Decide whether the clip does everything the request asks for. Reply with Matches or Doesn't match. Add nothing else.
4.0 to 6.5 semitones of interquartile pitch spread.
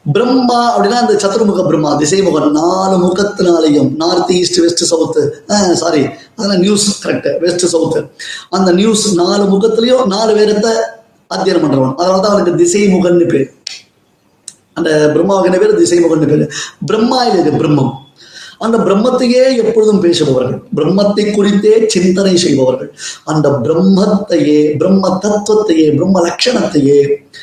Matches